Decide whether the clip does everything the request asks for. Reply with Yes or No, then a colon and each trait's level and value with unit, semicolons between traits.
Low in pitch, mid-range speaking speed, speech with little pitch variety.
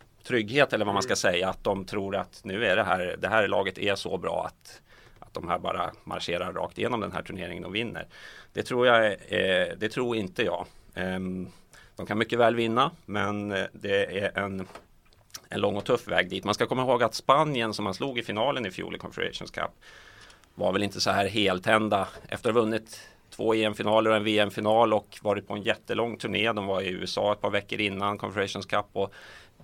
No: low, 105 Hz; fast, 210 wpm; narrow, 2.1 semitones